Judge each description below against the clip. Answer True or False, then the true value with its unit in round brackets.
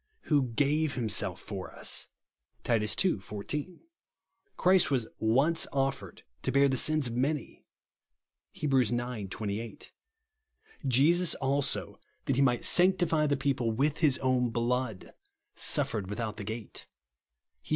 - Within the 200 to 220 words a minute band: False (140 wpm)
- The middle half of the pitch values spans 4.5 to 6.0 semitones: True (4.8 semitones)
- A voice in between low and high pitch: False (130 Hz)